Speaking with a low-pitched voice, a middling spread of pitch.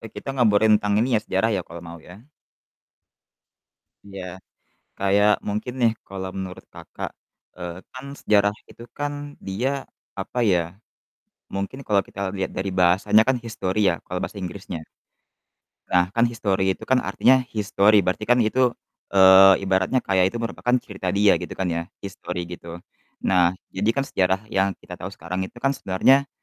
Yes: low, 100 Hz; average, 3.0 semitones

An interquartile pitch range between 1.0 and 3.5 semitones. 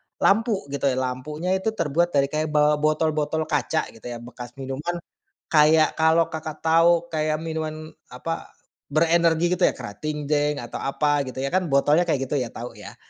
Yes: average, 2.9 semitones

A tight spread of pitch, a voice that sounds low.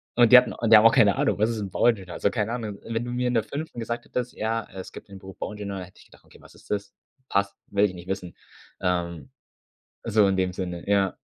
No: average, 3.1 semitones; low, 100 Hz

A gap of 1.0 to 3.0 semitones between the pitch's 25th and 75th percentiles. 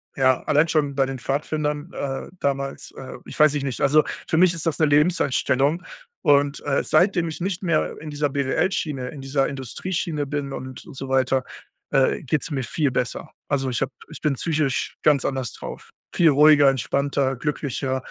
Yes: narrow, 2.4 semitones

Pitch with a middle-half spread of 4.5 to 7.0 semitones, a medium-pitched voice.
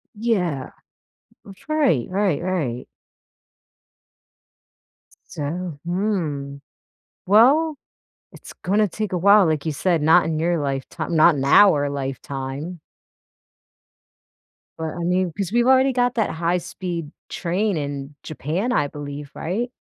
Yes: wide, 5.6 semitones; medium, 170 Hz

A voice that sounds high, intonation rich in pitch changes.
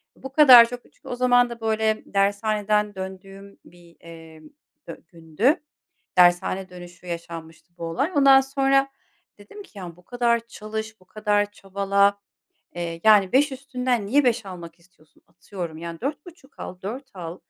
Yes: high, 205 Hz; wide, 5.7 semitones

